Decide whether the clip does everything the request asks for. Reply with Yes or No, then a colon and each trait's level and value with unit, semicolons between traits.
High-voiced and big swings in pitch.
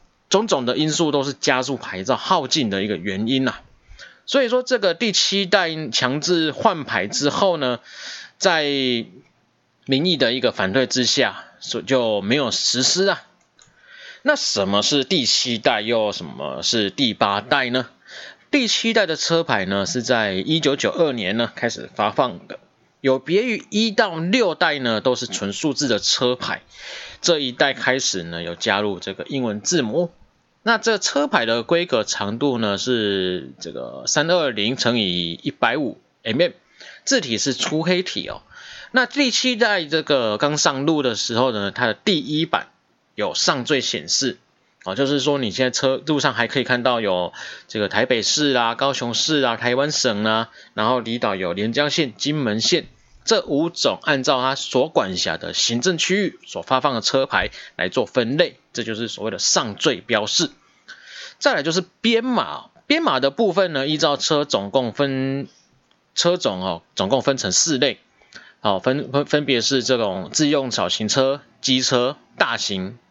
No: low, 135 Hz; wide, 5.9 semitones